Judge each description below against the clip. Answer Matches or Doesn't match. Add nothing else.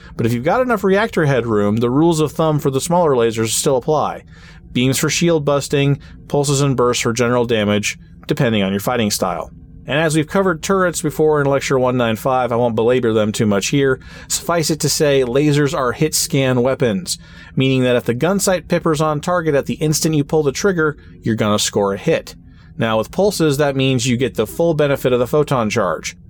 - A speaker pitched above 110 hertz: Matches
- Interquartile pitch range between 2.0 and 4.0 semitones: Doesn't match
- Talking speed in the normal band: Doesn't match